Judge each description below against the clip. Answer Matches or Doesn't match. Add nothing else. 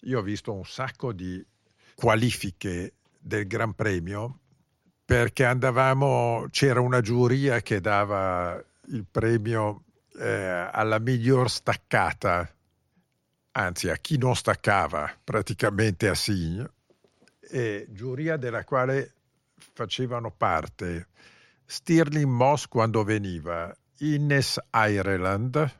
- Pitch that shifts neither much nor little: Matches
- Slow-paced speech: Matches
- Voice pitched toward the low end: Matches